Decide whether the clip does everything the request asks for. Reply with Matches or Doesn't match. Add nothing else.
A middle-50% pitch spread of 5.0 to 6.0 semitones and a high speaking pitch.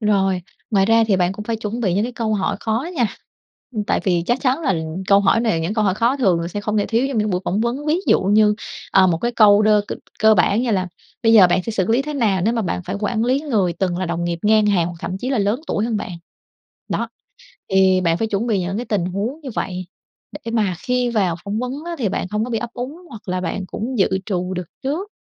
Doesn't match